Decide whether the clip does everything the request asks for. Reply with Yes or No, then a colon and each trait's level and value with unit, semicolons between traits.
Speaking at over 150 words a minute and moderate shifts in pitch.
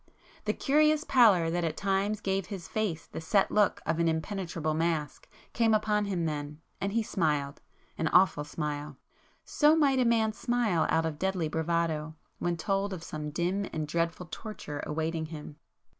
Yes: average, 165 wpm; average, 4.7 semitones